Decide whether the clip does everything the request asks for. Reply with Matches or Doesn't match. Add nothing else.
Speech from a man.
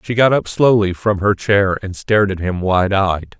Matches